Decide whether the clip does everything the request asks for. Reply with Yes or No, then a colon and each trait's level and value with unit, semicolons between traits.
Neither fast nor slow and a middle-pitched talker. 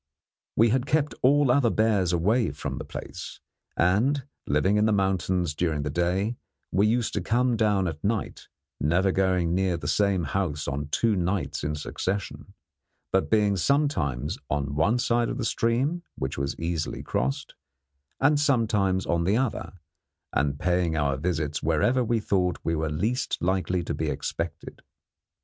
No: average, 160 wpm; very low, 95 Hz